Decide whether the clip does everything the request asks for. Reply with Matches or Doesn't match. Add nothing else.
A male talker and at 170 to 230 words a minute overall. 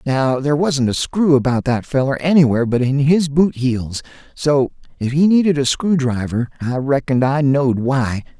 Matches